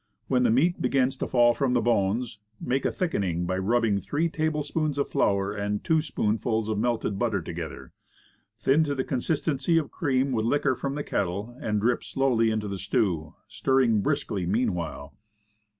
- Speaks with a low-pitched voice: Yes, low, 120 Hz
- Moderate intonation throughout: Yes, average, 5.0 semitones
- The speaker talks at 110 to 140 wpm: No, average, 175 wpm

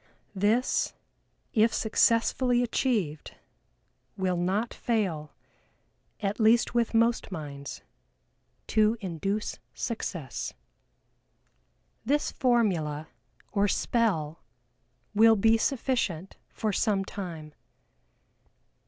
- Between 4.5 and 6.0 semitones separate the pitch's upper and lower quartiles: Yes, average, 4.8 semitones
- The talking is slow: Yes, slow, 80 wpm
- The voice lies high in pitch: Yes, high, 210 Hz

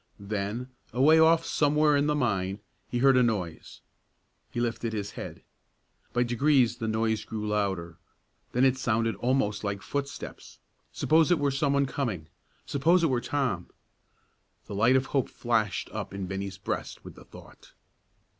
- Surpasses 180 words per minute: No, average, 160 wpm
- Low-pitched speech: Yes, low, 120 Hz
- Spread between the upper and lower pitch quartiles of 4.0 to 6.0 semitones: Yes, average, 5.1 semitones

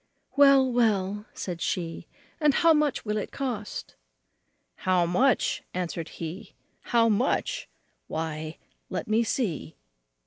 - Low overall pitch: No, high, 210 Hz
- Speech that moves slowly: Yes, slow, 115 wpm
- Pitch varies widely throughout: Yes, wide, 6.7 semitones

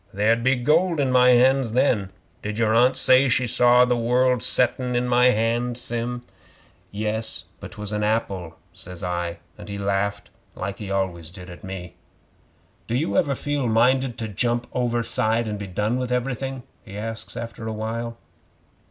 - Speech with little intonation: No, average, 3.4 semitones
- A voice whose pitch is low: Yes, low, 115 Hz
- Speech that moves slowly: No, average, 170 wpm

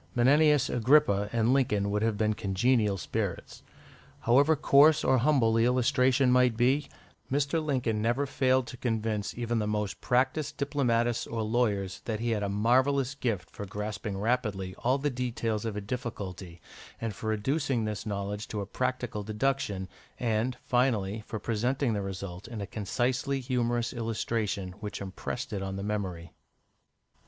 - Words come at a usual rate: Yes, average, 155 wpm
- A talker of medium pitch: No, low, 115 Hz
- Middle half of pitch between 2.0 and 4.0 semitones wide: Yes, average, 3.7 semitones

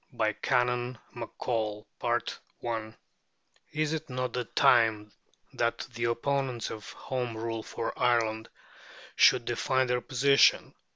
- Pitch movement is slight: Yes, narrow, 2.1 semitones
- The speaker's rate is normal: No, slow, 105 wpm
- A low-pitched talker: Yes, low, 120 Hz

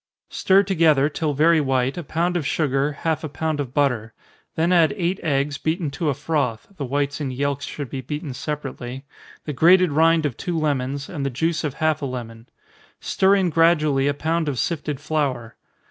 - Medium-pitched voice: Yes, medium, 150 Hz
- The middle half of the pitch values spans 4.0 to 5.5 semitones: No, average, 3.1 semitones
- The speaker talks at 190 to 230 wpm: Yes, average, 195 wpm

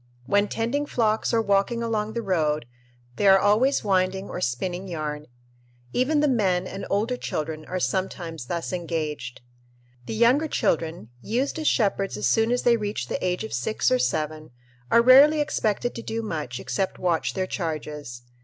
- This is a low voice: No, high, 195 Hz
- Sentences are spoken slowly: No, average, 170 wpm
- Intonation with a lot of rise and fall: Yes, wide, 6.4 semitones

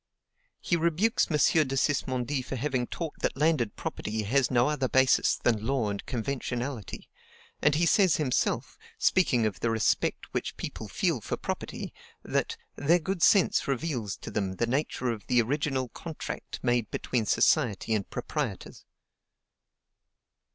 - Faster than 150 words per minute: No, average, 145 wpm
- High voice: No, low, 130 Hz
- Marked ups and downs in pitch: No, average, 4.4 semitones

